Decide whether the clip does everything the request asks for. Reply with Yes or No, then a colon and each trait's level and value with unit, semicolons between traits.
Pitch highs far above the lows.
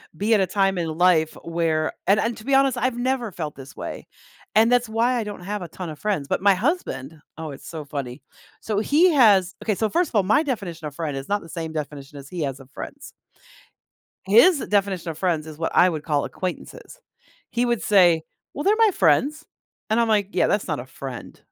Yes: wide, 6.4 semitones